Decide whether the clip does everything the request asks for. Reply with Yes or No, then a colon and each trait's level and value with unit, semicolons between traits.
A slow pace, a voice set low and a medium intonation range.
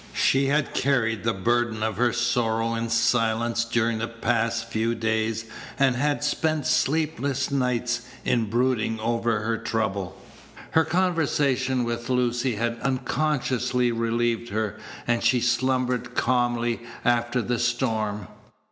No: slow, 130 wpm; low, 120 Hz; narrow, 1.9 semitones